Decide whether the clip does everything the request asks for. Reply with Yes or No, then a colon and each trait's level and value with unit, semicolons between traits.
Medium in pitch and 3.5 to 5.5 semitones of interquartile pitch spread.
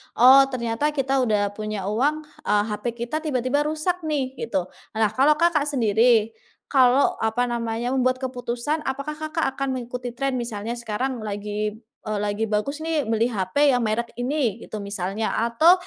No: high, 245 Hz; average, 3.9 semitones